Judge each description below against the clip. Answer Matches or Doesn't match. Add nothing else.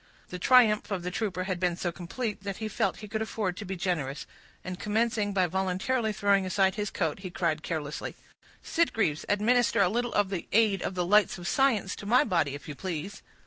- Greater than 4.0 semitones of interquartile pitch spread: Doesn't match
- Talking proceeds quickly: Matches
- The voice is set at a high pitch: Matches